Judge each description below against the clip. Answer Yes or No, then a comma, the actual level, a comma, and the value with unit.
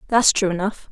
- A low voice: No, high, 200 Hz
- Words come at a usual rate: Yes, average, 195 wpm